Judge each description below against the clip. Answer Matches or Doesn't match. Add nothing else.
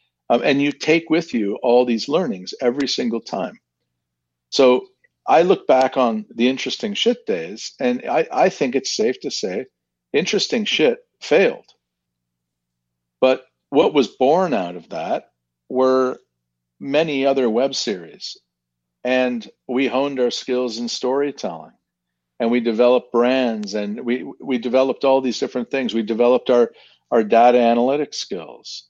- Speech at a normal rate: Matches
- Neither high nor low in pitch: Doesn't match